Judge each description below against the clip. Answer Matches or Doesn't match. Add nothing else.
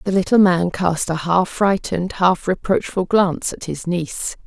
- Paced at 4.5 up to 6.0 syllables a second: Matches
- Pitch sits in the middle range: Matches